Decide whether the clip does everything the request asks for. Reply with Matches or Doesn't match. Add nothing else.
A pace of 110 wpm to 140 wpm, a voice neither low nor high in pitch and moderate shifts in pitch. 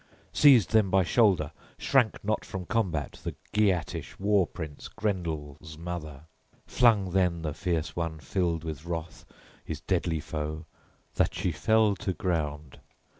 Doesn't match